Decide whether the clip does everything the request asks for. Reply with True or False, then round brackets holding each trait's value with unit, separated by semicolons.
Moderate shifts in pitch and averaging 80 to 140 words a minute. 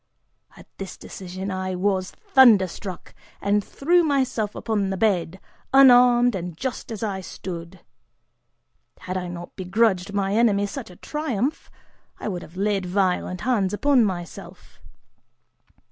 True (4.1 semitones; 135 wpm)